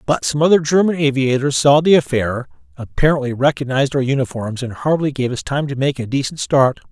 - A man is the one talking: Yes, male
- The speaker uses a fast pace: No, average, 190 wpm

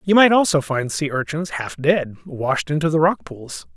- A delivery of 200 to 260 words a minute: Yes, fast, 205 wpm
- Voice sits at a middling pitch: Yes, medium, 155 Hz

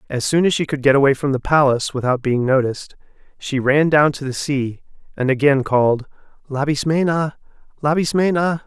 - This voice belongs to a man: Yes, male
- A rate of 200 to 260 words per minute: No, average, 165 wpm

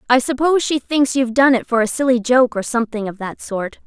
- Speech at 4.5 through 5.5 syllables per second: No, 6.1 syllables/s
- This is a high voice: Yes, high, 245 Hz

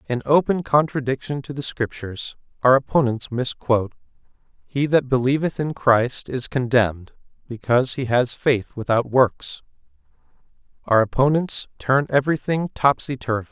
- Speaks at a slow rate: Yes, slow, 125 wpm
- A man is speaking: Yes, male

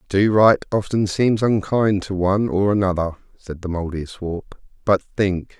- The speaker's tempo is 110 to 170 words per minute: Yes, average, 160 wpm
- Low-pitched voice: Yes, very low, 95 Hz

